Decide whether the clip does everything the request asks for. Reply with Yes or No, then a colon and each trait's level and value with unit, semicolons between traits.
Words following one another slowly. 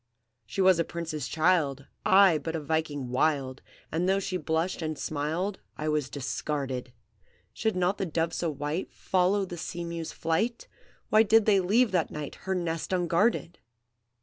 No: average, 165 wpm